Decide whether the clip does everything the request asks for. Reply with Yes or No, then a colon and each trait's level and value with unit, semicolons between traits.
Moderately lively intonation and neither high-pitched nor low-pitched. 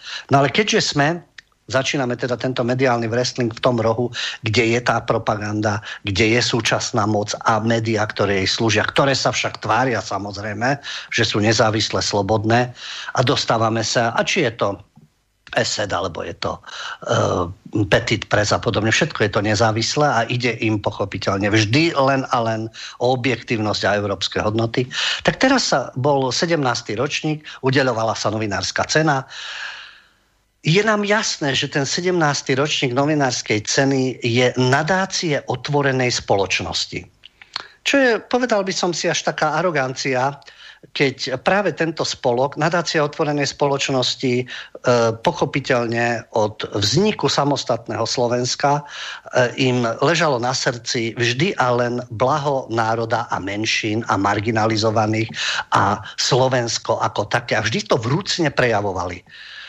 No: average, 4.1 semitones; low, 125 Hz